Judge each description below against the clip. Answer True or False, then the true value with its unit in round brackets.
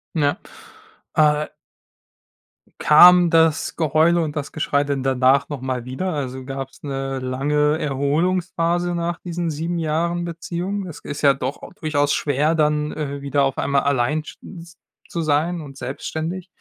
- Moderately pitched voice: True (150 Hz)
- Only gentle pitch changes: False (3.3 semitones)